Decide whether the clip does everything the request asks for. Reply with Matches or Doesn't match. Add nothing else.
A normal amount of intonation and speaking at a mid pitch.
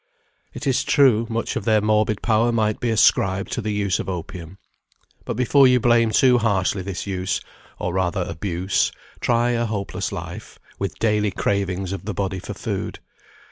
Doesn't match